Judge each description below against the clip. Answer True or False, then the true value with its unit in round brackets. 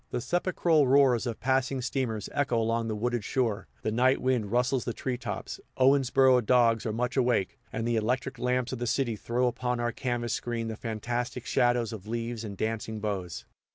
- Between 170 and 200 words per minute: True (190 wpm)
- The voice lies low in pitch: True (120 Hz)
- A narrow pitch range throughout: True (2.2 semitones)